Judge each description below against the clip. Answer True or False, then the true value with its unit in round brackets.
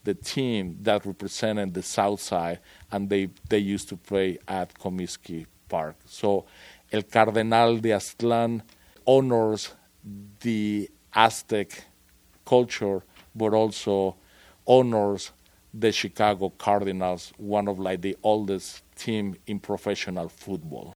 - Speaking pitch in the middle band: False (100 Hz)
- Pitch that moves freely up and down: False (2.5 semitones)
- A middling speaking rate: False (115 wpm)